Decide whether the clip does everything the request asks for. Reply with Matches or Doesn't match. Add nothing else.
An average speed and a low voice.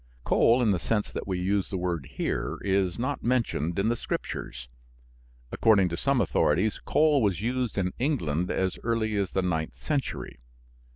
Matches